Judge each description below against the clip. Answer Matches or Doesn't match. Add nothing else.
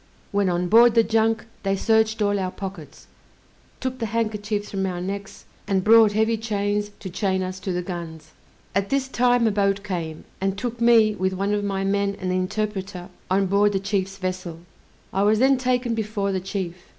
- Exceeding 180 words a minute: Matches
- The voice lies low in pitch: Doesn't match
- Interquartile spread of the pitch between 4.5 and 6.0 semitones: Doesn't match